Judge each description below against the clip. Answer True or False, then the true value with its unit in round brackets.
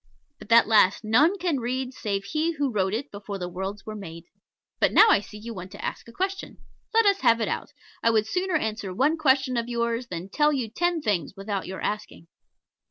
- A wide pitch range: True (6.4 semitones)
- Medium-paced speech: False (220 wpm)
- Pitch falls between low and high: False (230 Hz)